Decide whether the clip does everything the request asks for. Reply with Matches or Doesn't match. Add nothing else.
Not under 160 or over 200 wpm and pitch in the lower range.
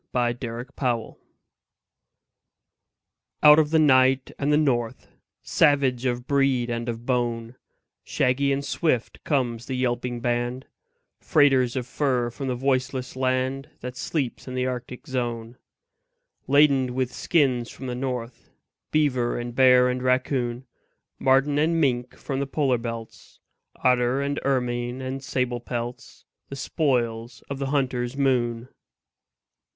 Doesn't match